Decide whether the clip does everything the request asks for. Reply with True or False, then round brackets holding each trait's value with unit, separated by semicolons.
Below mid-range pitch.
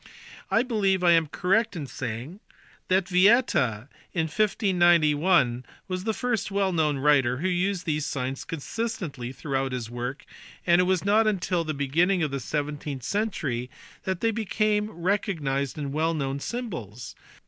False (165 Hz)